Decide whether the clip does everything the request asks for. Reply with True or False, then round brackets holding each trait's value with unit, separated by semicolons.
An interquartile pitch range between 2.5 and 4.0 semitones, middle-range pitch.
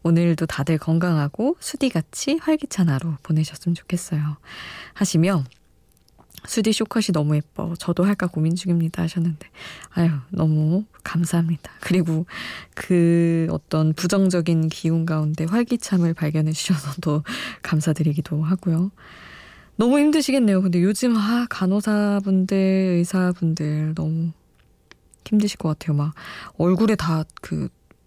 True (3.5 semitones; 170 Hz)